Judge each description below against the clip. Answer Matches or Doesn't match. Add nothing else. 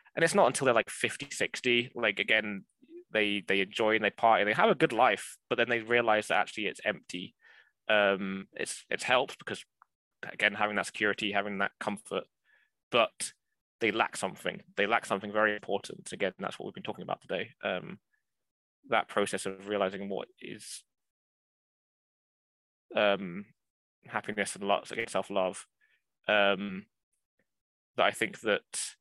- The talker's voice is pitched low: Matches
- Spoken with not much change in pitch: Matches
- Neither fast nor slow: Matches